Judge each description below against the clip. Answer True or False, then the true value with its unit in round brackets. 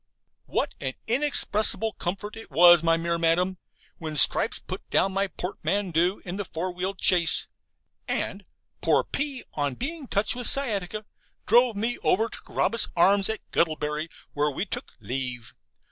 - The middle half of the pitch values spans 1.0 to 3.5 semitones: False (4.8 semitones)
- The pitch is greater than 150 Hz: True (185 Hz)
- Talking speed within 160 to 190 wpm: False (145 wpm)